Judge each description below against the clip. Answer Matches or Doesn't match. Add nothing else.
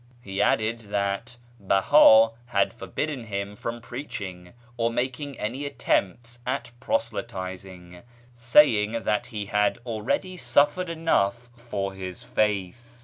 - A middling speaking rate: Doesn't match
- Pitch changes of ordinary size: Matches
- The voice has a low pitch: Matches